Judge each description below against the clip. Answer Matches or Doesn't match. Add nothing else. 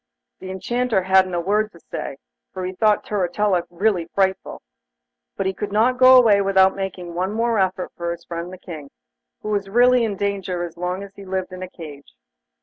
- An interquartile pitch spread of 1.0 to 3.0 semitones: Matches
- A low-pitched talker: Doesn't match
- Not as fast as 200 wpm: Doesn't match